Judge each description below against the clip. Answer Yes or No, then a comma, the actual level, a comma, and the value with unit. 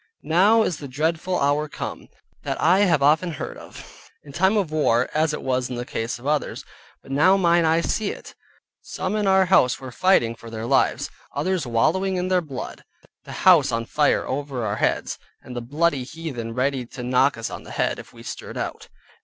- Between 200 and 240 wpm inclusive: Yes, fast, 205 wpm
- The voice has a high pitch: No, medium, 150 Hz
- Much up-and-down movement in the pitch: Yes, wide, 6.1 semitones